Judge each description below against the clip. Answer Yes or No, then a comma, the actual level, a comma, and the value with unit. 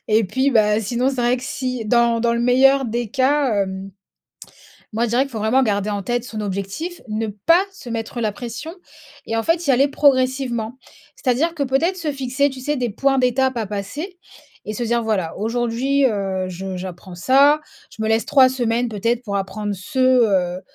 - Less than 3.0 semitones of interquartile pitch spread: No, average, 3.8 semitones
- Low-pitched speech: No, high, 240 Hz